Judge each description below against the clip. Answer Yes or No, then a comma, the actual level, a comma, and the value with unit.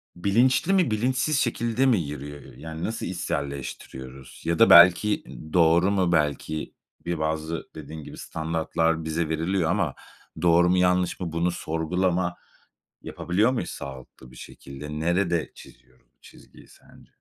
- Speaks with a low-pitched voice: Yes, very low, 85 Hz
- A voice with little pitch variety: No, average, 3.2 semitones